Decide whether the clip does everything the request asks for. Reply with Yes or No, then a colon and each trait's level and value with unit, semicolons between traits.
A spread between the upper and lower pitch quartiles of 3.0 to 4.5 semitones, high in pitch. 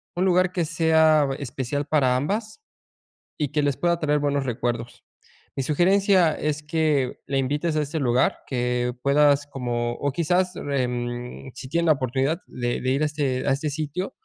No: average, 3.6 semitones; medium, 145 Hz